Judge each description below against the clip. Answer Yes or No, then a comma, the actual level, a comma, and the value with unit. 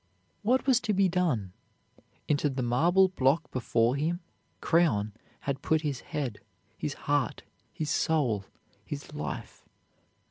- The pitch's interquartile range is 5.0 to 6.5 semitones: Yes, wide, 5.5 semitones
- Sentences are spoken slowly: Yes, slow, 130 wpm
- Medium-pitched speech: Yes, medium, 150 Hz